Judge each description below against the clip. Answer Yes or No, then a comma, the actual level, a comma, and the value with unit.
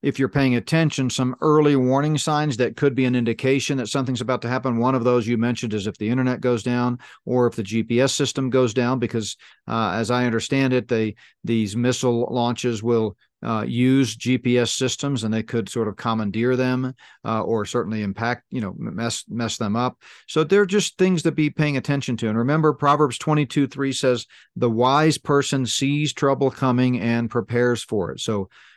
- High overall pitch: No, low, 125 Hz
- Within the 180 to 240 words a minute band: Yes, average, 195 wpm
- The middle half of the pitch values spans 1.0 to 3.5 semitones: Yes, average, 2.8 semitones